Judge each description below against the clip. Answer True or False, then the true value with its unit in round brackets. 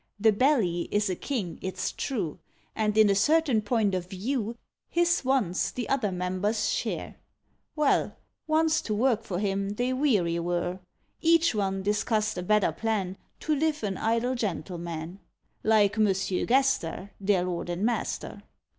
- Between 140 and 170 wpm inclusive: True (150 wpm)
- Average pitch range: True (5.0 semitones)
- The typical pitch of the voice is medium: False (210 Hz)